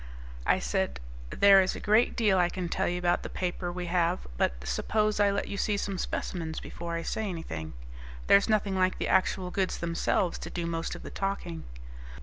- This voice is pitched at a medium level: Yes, medium, 180 Hz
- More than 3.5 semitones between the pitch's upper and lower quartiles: No, average, 2.9 semitones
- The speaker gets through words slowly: No, average, 200 wpm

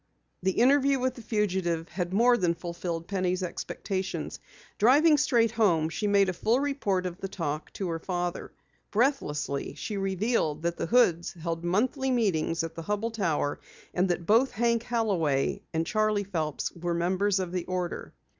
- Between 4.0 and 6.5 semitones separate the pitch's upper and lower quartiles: Yes, average, 4.8 semitones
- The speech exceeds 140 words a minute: Yes, average, 165 wpm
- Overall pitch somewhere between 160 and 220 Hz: Yes, high, 190 Hz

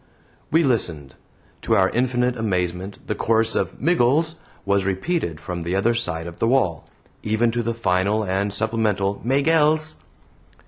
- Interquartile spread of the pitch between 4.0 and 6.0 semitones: Yes, average, 4.7 semitones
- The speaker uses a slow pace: No, average, 145 wpm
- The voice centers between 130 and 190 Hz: No, low, 110 Hz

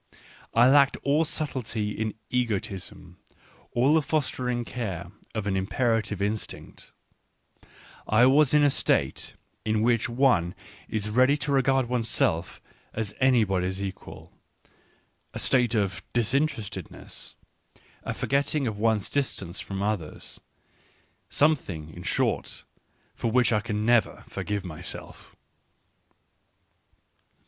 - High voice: No, low, 115 Hz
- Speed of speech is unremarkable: No, slow, 115 wpm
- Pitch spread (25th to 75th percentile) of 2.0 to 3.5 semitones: No, average, 4.7 semitones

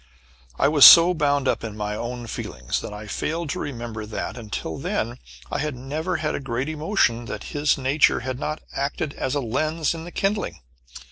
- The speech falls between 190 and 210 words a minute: Yes, average, 195 wpm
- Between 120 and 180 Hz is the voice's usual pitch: Yes, medium, 140 Hz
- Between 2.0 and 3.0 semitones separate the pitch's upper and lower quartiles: No, average, 4.8 semitones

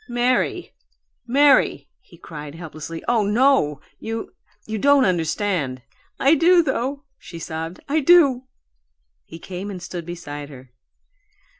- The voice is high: Yes, high, 200 Hz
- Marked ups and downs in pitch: Yes, wide, 8.5 semitones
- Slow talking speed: Yes, slow, 125 wpm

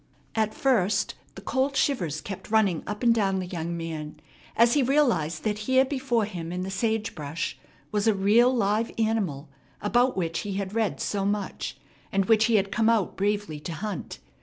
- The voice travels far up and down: No, average, 3.9 semitones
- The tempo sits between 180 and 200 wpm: Yes, average, 185 wpm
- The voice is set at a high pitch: Yes, high, 205 Hz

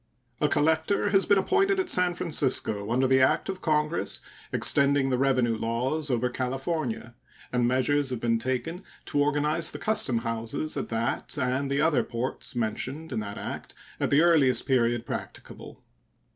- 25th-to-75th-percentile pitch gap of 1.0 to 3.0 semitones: No, average, 4.6 semitones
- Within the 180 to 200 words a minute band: No, average, 160 wpm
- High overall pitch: No, low, 135 Hz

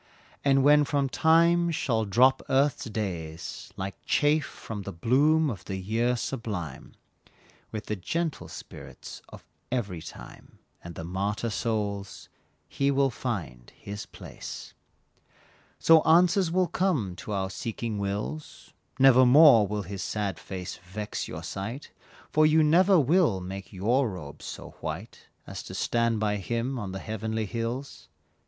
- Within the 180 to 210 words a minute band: No, average, 140 wpm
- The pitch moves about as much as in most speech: No, wide, 6.3 semitones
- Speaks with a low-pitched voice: Yes, low, 115 Hz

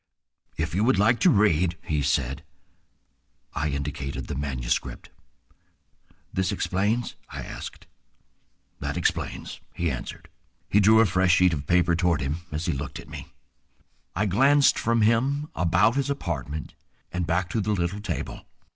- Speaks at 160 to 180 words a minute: No, average, 150 wpm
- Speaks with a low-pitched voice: Yes, very low, 90 Hz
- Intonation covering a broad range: Yes, wide, 5.8 semitones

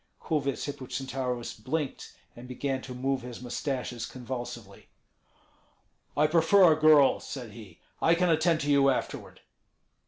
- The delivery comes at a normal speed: No, slow, 130 wpm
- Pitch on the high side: No, low, 135 Hz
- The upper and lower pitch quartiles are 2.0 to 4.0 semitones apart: Yes, average, 3.5 semitones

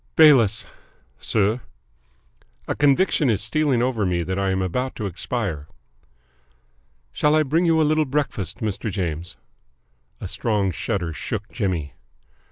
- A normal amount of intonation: No, wide, 6.7 semitones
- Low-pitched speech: Yes, low, 110 Hz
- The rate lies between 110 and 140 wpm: Yes, slow, 135 wpm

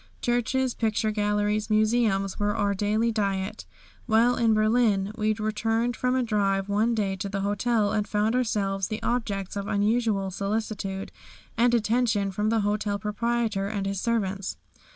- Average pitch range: No, narrow, 2.3 semitones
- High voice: Yes, high, 210 Hz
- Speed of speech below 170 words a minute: Yes, average, 150 wpm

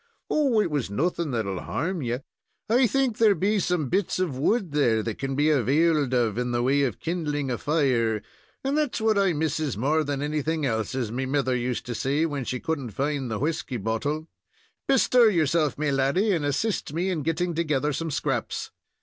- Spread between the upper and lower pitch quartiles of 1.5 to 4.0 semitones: No, average, 4.7 semitones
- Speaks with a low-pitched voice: No, medium, 150 Hz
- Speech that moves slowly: No, average, 200 wpm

